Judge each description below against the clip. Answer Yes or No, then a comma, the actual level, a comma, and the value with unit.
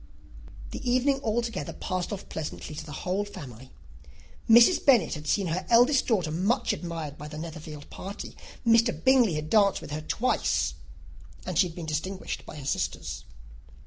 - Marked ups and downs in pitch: Yes, wide, 7.0 semitones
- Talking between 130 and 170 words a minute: Yes, average, 165 wpm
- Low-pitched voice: No, medium, 185 Hz